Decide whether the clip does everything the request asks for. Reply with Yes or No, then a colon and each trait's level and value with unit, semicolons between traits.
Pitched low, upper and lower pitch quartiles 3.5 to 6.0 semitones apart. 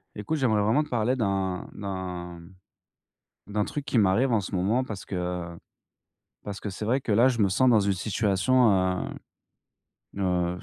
Yes: low, 100 Hz; average, 3.9 semitones